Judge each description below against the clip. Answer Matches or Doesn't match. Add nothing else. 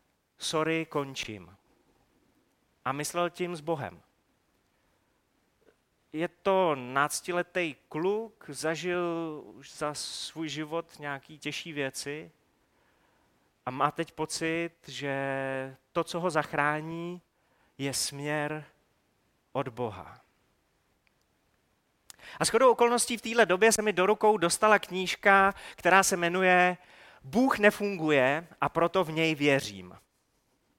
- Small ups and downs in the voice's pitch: Doesn't match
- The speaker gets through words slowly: Matches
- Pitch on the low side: Doesn't match